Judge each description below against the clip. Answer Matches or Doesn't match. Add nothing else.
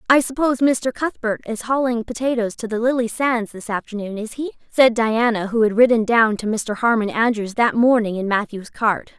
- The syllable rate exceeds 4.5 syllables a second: Matches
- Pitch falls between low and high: Doesn't match